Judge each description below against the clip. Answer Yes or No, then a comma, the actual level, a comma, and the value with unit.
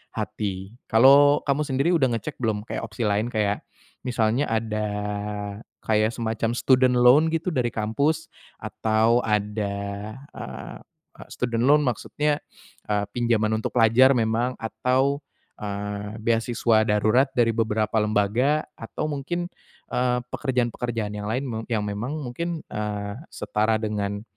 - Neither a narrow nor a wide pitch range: Yes, average, 3.4 semitones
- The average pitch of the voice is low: Yes, low, 115 Hz